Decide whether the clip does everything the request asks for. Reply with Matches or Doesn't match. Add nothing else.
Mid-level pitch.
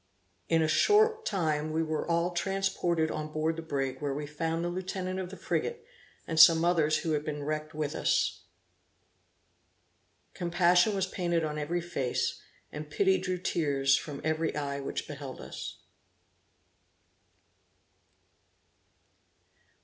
Matches